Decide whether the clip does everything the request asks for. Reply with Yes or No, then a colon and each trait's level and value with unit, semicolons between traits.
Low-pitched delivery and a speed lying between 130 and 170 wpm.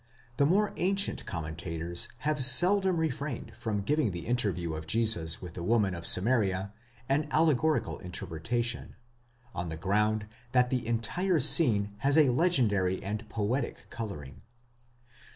Yes: low, 115 Hz; slow, 135 wpm